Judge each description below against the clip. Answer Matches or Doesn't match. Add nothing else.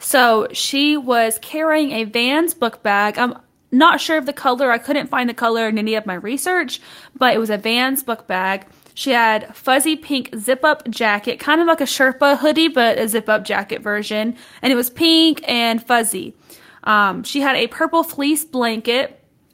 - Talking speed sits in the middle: Matches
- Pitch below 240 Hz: Doesn't match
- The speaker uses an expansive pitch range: Doesn't match